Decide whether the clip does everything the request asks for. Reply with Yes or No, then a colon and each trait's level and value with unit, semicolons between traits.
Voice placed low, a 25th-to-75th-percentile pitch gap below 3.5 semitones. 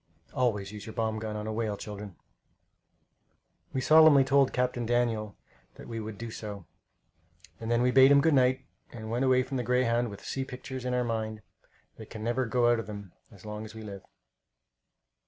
Yes: low, 115 Hz; average, 2.9 semitones